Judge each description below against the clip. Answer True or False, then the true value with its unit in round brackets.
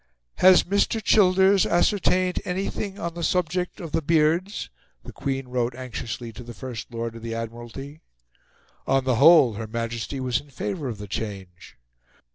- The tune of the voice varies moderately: False (7.4 semitones)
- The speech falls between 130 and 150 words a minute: False (160 wpm)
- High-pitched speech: False (135 Hz)